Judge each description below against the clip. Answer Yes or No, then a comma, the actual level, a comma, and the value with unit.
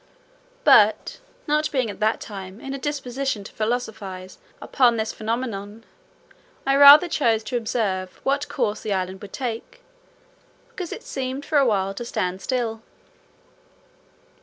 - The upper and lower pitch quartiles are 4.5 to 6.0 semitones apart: Yes, average, 4.9 semitones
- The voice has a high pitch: Yes, high, 230 Hz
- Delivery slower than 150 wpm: Yes, average, 140 wpm